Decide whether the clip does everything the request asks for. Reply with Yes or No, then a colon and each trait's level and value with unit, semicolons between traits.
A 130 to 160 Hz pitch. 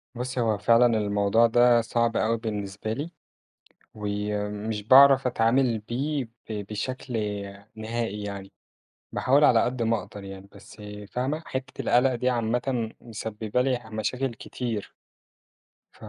No: low, 115 Hz